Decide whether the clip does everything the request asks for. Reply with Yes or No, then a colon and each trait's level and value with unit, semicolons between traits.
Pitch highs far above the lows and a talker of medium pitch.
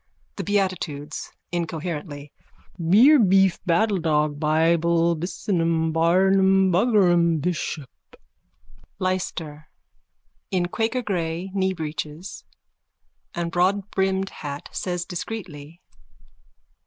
No: average, 3.0 semitones; medium, 175 Hz